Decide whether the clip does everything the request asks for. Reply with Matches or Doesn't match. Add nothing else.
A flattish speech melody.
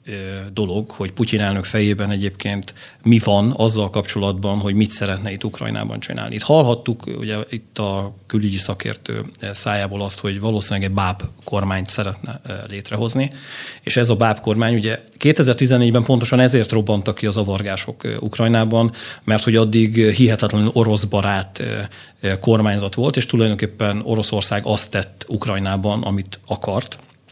Matches